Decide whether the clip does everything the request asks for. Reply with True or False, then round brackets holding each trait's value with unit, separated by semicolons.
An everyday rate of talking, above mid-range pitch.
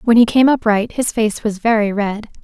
False (220 wpm; 220 Hz)